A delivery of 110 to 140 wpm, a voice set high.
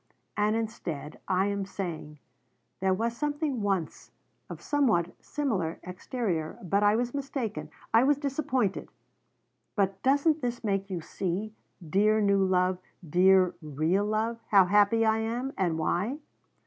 Yes: slow, 135 wpm; high, 205 Hz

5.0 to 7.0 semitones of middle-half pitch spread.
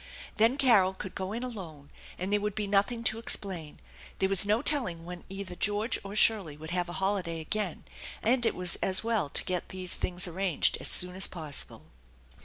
No: average, 3.3 semitones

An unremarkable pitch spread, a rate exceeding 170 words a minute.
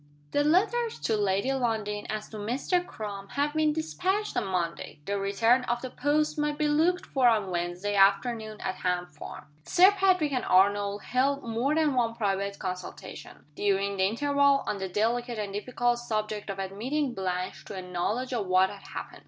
No: wide, 6.2 semitones; average, 180 wpm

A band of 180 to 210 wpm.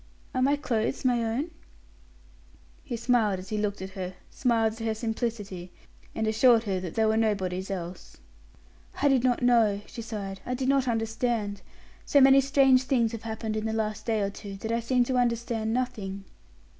Yes: average, 185 wpm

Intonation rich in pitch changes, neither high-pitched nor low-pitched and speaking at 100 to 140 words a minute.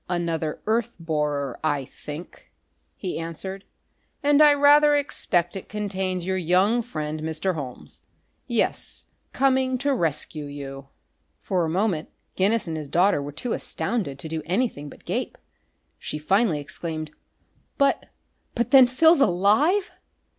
Yes: wide, 7.4 semitones; medium, 180 Hz; slow, 135 wpm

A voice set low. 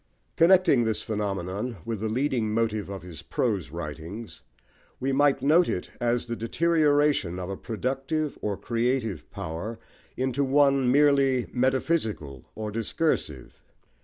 Yes: low, 120 Hz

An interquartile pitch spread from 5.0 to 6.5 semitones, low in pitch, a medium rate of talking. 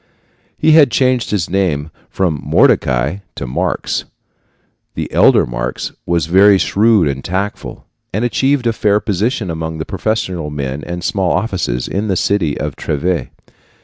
Yes: wide, 5.6 semitones; very low, 95 Hz; average, 145 wpm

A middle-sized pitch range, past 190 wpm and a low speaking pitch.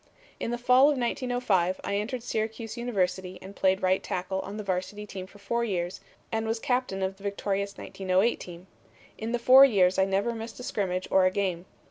No: average, 3.8 semitones; average, 200 wpm; high, 200 Hz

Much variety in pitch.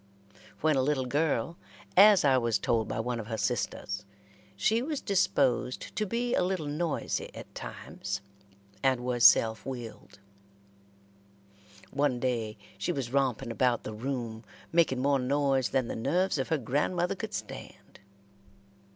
No: average, 4.8 semitones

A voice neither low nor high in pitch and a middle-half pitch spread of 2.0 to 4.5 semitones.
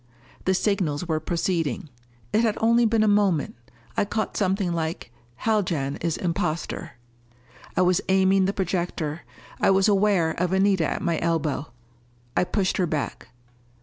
Yes: medium, 180 Hz; average, 3.2 semitones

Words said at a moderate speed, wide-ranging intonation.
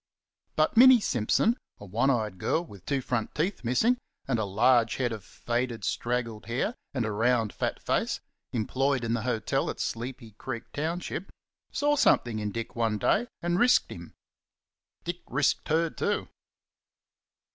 Yes: average, 155 wpm; wide, 5.8 semitones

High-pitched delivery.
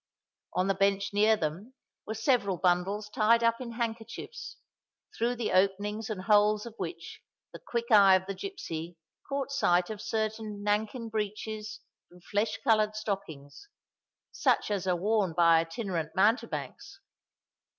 Yes: high, 210 Hz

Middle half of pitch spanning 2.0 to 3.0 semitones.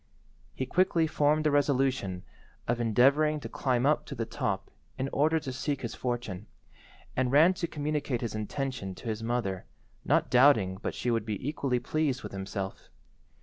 No: average, 4.5 semitones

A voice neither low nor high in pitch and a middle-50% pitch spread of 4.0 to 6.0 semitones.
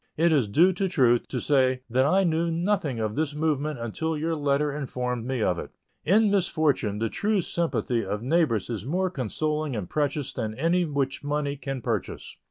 Yes: medium, 145 Hz; average, 4.7 semitones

